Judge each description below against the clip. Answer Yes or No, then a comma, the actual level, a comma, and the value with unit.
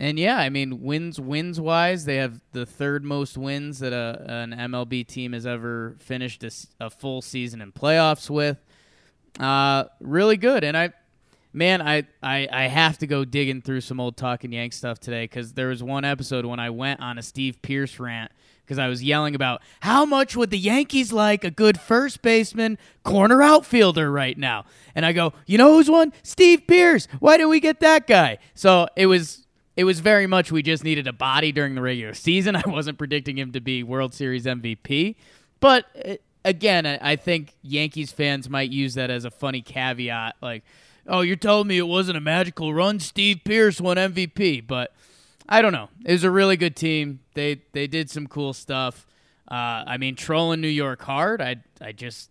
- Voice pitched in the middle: Yes, medium, 145 Hz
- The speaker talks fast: No, average, 195 wpm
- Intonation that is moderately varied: No, wide, 6.1 semitones